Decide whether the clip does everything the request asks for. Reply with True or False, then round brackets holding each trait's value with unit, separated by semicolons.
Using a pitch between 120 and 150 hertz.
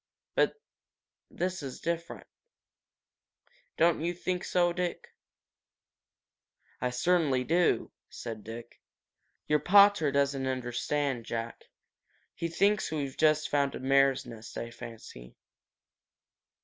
True (140 Hz)